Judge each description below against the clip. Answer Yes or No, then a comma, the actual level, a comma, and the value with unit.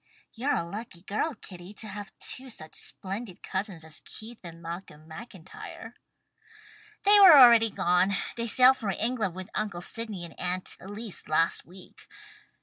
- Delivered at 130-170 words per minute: Yes, average, 150 wpm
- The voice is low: No, high, 200 Hz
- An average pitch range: Yes, average, 4.7 semitones